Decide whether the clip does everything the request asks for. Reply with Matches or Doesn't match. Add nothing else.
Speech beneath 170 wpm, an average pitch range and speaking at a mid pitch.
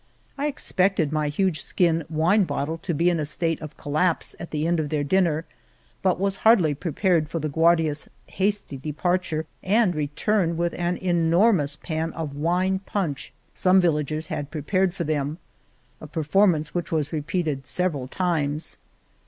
Matches